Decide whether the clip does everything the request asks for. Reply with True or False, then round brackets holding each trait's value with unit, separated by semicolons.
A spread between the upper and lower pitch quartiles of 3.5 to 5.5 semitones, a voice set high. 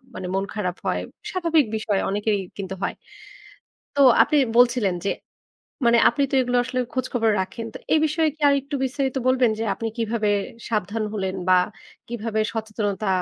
True (3.8 semitones; 225 Hz)